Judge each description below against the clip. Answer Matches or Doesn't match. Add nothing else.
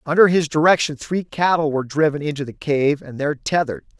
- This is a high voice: Doesn't match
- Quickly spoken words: Doesn't match